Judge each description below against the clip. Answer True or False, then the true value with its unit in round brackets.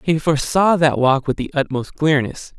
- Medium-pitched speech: True (145 Hz)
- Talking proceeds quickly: False (185 wpm)